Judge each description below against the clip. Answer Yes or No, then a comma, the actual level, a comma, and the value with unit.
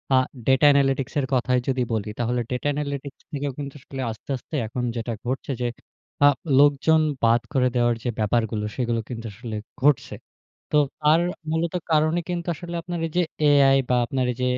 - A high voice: No, low, 135 Hz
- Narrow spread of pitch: No, average, 3.3 semitones